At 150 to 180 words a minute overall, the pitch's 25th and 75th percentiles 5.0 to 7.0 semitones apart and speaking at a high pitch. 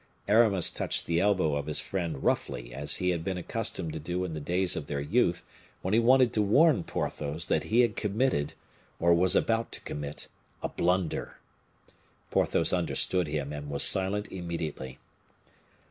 No: average, 170 wpm; average, 5.3 semitones; very low, 90 Hz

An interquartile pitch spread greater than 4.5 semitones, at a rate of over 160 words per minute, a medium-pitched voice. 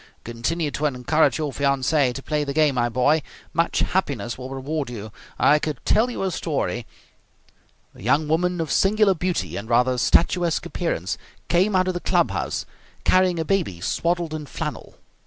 Yes: average, 5.2 semitones; average, 175 wpm; medium, 150 Hz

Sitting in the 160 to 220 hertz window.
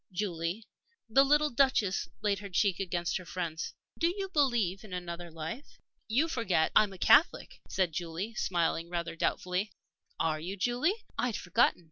Yes: high, 190 Hz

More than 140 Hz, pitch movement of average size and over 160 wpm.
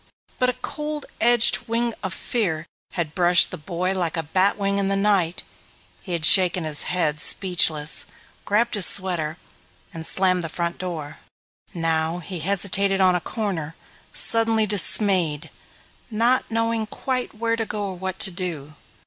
No: medium, 185 Hz; average, 4.2 semitones; average, 155 wpm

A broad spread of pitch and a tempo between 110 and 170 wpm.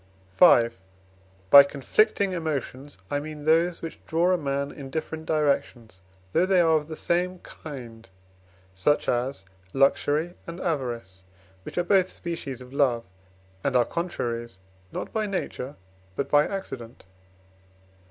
No: average, 5.0 semitones; slow, 135 wpm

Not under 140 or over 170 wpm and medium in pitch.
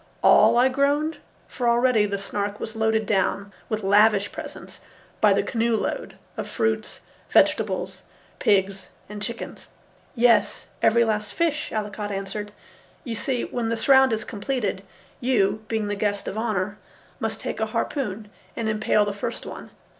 No: average, 155 wpm; high, 220 Hz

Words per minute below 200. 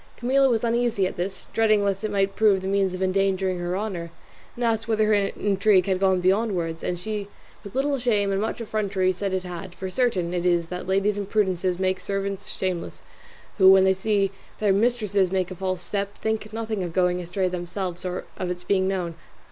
No: fast, 205 wpm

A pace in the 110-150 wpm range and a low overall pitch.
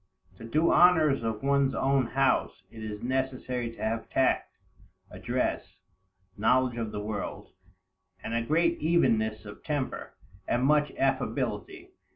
Yes: average, 140 wpm; low, 130 Hz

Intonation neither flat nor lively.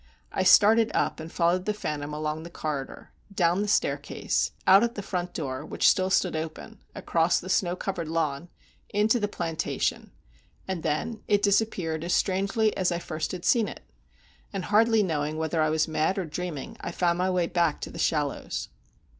Yes: average, 3.9 semitones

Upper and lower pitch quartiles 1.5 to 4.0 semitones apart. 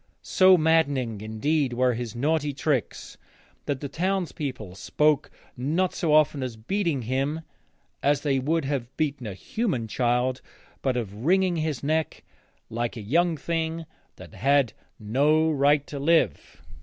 No: average, 4.6 semitones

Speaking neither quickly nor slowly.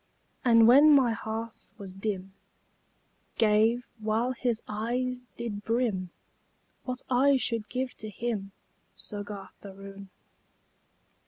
No: slow, 105 wpm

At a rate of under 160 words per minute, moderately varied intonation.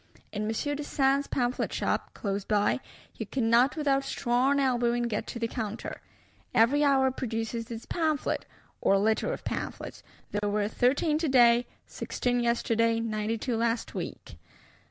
Yes: average, 140 wpm; average, 3.2 semitones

